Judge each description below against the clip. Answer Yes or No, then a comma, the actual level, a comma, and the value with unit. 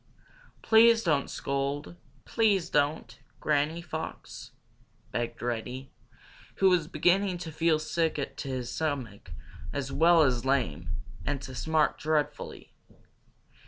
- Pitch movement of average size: Yes, average, 4.1 semitones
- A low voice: No, medium, 150 Hz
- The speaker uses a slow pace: Yes, slow, 115 wpm